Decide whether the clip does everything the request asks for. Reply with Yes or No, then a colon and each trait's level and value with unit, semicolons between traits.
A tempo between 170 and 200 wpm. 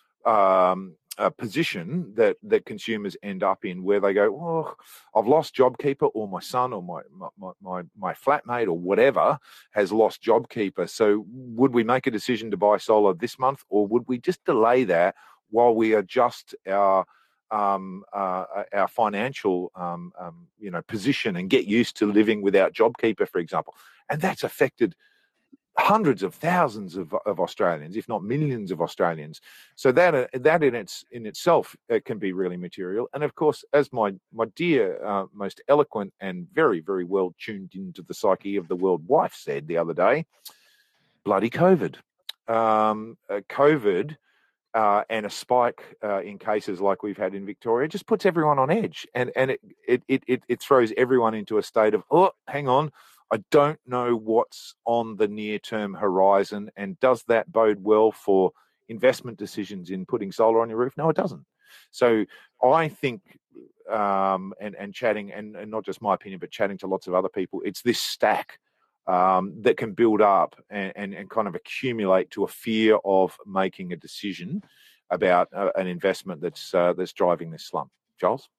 Yes: average, 180 wpm